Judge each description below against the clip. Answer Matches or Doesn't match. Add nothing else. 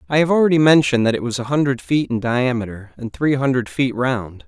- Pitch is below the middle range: Matches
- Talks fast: Matches